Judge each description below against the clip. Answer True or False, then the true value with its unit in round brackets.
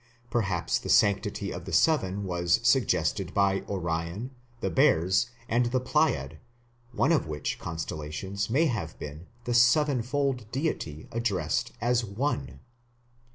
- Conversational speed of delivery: False (120 wpm)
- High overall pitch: False (100 Hz)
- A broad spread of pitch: True (6.5 semitones)